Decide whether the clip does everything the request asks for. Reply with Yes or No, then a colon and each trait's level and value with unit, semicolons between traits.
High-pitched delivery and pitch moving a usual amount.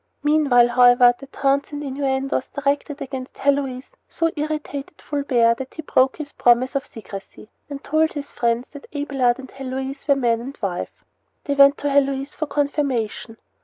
No: very high, 275 Hz; narrow, 2.3 semitones